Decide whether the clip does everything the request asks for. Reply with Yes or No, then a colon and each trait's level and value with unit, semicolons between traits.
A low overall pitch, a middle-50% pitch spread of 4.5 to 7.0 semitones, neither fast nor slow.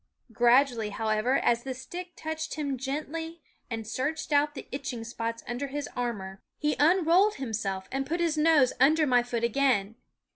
No: very high, 265 Hz; average, 4.9 semitones; average, 160 wpm